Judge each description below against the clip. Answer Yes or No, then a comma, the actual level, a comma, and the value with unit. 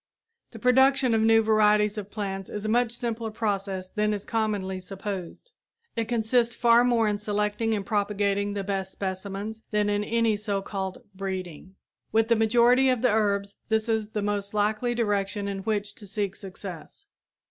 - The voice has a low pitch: No, high, 210 Hz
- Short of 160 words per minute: No, average, 170 wpm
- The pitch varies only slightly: Yes, narrow, 2.0 semitones